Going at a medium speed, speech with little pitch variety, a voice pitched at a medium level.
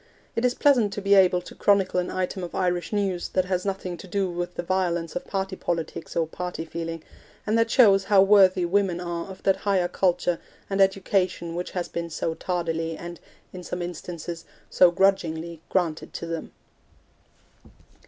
Yes: average, 180 wpm; narrow, 2.2 semitones; medium, 180 Hz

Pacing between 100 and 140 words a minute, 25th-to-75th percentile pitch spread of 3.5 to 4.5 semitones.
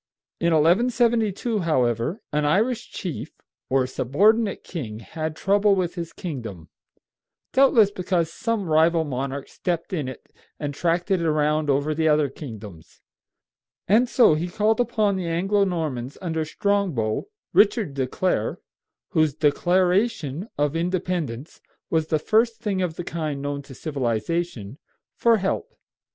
No: slow, 135 wpm; wide, 5.5 semitones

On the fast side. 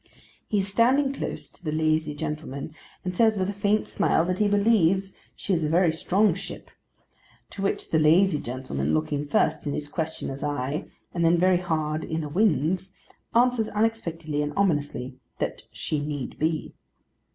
No: average, 170 wpm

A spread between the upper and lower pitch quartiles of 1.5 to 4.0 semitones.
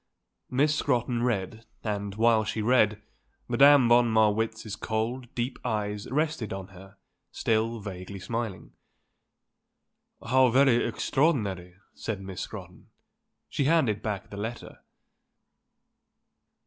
Yes: average, 3.3 semitones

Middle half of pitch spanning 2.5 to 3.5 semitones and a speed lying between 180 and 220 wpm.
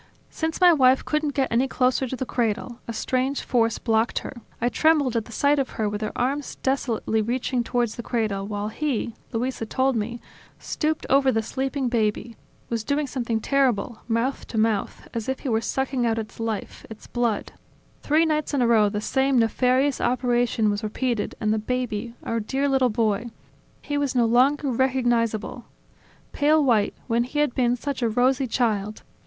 Yes: average, 3.0 semitones; average, 185 wpm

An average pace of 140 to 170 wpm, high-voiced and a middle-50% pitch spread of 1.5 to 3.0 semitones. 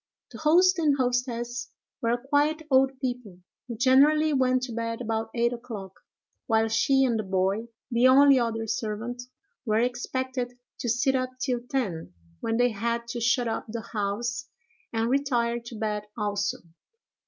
Yes: average, 155 wpm; high, 240 Hz; narrow, 2.6 semitones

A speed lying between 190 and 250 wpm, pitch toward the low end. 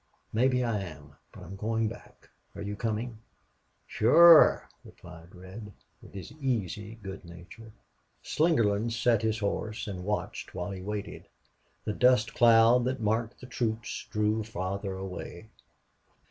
No: slow, 135 wpm; low, 110 Hz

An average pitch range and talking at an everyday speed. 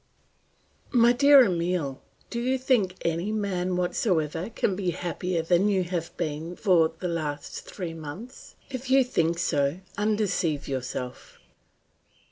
No: average, 4.7 semitones; slow, 130 wpm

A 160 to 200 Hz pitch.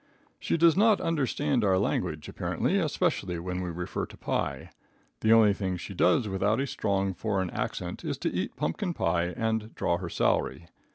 No: low, 100 Hz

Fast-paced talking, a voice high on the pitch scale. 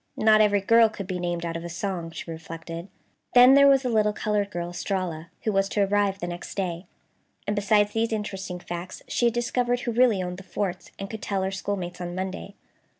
Yes: fast, 215 wpm; high, 195 Hz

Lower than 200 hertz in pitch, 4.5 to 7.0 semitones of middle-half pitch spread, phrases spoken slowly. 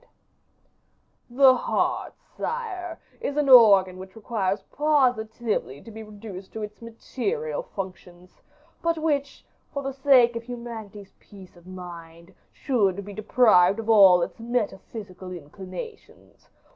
No: high, 220 Hz; wide, 5.4 semitones; slow, 120 wpm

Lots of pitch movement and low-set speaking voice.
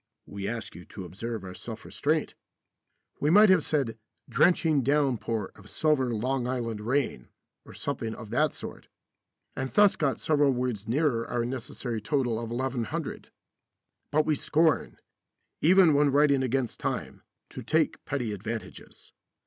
No: average, 4.5 semitones; low, 130 Hz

